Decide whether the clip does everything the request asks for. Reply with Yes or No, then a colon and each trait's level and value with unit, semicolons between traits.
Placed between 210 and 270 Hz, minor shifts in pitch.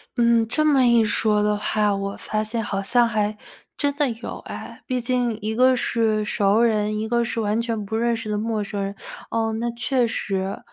Yes: high, 225 Hz; narrow, 2.1 semitones